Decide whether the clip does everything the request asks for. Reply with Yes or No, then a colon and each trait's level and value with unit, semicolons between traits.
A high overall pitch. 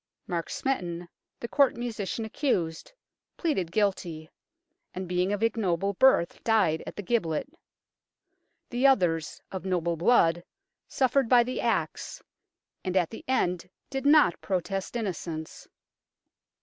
Yes: high, 195 Hz